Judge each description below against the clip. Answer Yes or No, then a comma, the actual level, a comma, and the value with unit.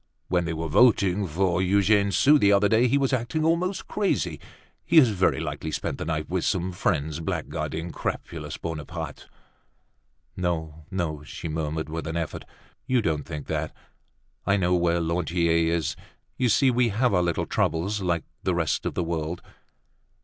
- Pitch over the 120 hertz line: No, very low, 90 Hz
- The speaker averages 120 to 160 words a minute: No, average, 170 wpm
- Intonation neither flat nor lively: Yes, average, 4.1 semitones